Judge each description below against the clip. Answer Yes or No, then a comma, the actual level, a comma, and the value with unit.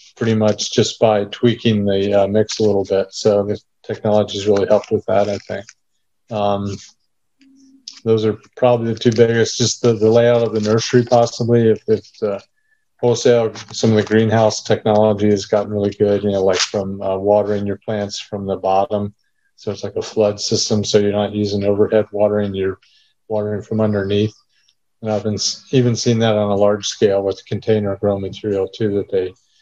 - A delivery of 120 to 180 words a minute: No, average, 190 wpm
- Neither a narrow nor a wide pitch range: No, narrow, 1.9 semitones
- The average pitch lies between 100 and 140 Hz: Yes, low, 105 Hz